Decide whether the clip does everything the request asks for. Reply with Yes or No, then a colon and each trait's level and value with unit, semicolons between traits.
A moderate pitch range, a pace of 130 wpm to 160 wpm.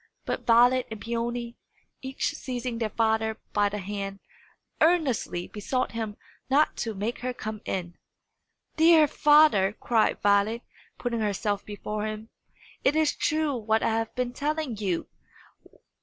Yes: average, 3.5 semitones; average, 140 wpm